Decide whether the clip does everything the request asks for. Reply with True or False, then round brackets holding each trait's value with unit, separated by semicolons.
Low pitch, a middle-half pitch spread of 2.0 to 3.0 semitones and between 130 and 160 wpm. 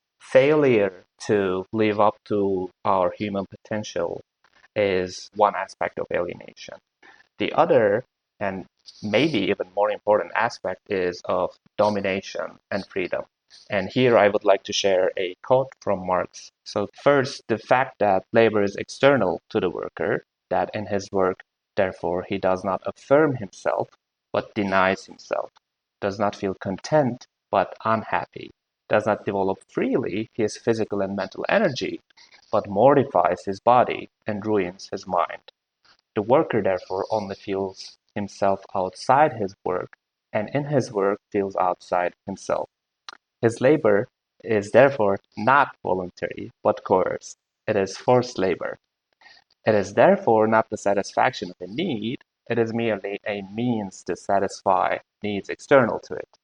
True (100 Hz; 2.6 semitones; 140 wpm)